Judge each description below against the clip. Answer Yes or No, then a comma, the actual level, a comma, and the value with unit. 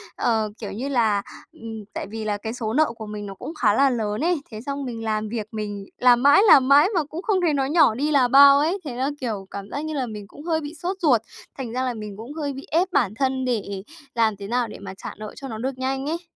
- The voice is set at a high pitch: Yes, very high, 250 Hz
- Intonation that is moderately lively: Yes, average, 4.8 semitones